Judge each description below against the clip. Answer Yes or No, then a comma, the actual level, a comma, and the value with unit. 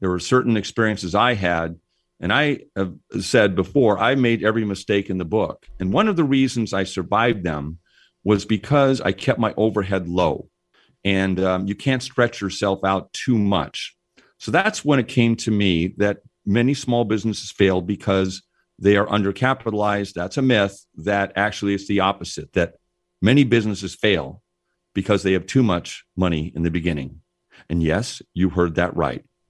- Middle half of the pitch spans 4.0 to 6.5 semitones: No, average, 3.3 semitones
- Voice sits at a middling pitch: No, low, 100 Hz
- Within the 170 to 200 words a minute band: Yes, average, 175 wpm